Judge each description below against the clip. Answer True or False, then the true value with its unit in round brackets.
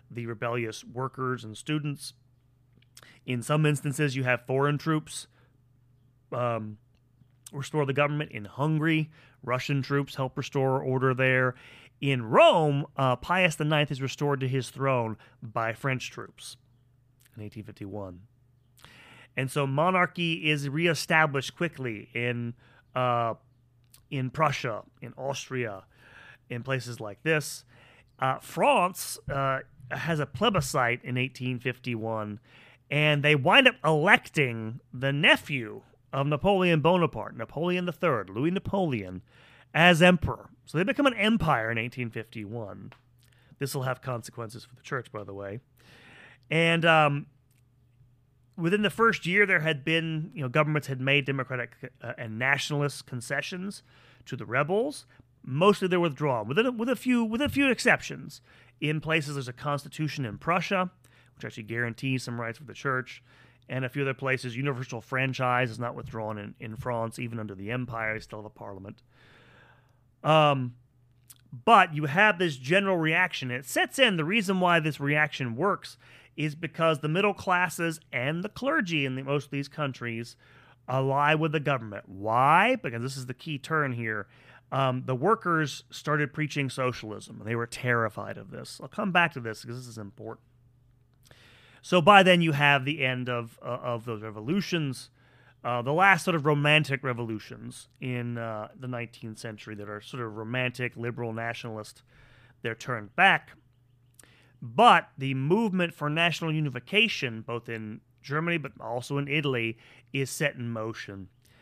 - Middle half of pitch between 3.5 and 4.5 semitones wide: True (3.9 semitones)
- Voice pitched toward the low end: True (130 Hz)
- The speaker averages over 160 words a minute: False (150 wpm)